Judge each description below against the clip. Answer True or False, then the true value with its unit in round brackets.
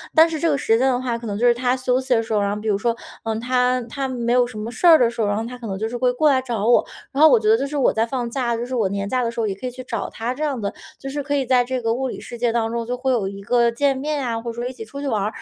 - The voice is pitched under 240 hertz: False (245 Hz)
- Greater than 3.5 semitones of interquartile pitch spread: False (2.5 semitones)